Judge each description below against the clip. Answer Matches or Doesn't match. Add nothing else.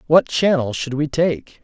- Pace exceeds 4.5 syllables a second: Doesn't match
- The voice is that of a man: Matches